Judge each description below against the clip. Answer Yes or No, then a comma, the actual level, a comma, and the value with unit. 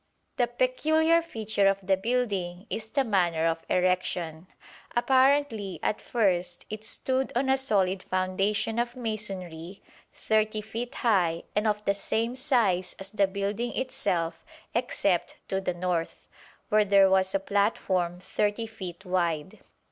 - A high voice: Yes, high, 200 Hz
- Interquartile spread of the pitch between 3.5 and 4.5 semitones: Yes, average, 4.0 semitones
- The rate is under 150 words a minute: Yes, average, 140 wpm